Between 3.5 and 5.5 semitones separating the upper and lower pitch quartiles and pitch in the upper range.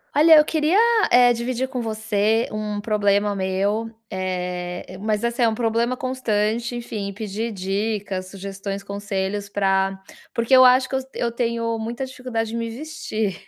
No: average, 3.1 semitones; high, 220 Hz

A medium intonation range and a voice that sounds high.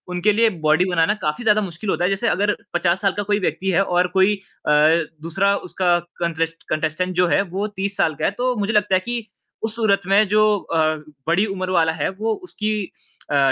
Yes: average, 3.4 semitones; high, 195 Hz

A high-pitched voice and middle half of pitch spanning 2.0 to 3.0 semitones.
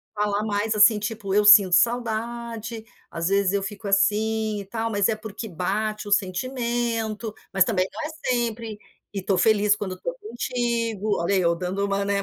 Yes: high, 210 Hz; narrow, 2.4 semitones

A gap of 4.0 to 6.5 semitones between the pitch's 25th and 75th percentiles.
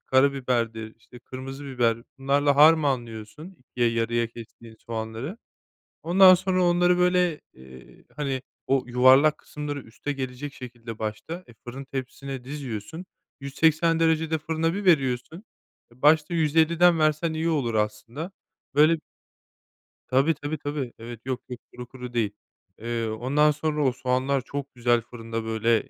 Yes: average, 4.8 semitones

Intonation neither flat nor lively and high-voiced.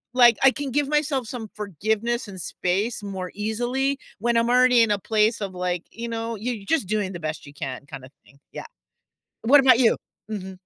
Yes: average, 4.4 semitones; high, 220 Hz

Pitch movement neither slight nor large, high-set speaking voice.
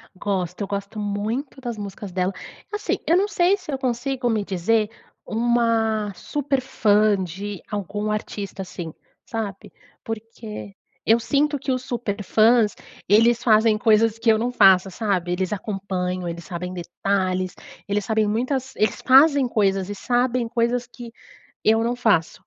Yes: average, 3.5 semitones; high, 215 Hz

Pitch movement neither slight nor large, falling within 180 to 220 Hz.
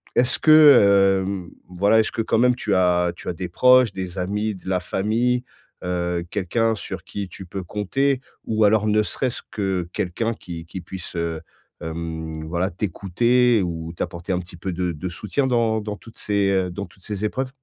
No: average, 3.9 semitones; very low, 95 Hz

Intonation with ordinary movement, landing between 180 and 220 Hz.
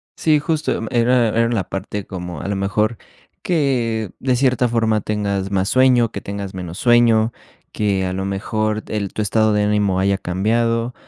No: average, 3.2 semitones; low, 110 Hz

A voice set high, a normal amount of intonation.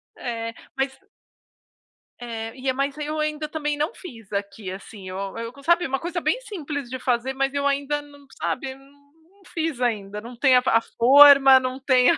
Yes: very high, 270 Hz; average, 3.5 semitones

